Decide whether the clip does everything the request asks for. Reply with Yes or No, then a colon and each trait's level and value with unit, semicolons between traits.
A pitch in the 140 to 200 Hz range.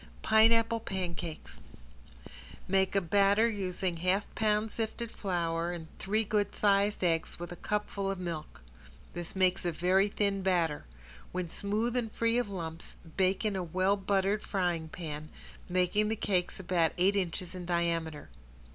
Yes: high, 190 Hz